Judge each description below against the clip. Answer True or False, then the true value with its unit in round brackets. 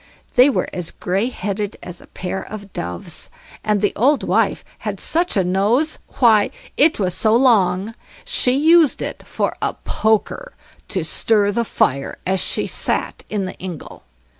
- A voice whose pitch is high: True (210 Hz)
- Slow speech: False (165 wpm)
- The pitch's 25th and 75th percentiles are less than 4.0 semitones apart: False (4.9 semitones)